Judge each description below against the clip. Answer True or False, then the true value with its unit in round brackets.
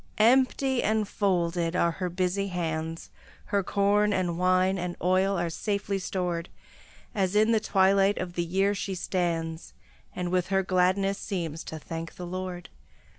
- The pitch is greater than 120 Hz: True (185 Hz)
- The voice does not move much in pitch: True (2.3 semitones)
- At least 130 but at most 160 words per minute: True (155 wpm)